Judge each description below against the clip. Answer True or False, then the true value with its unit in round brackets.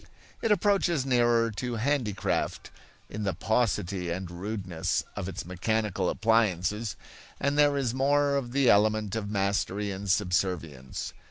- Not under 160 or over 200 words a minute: False (135 wpm)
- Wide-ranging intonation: False (4.6 semitones)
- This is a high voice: False (105 Hz)